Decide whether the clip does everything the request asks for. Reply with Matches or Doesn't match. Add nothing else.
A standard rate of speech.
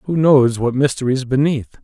Matches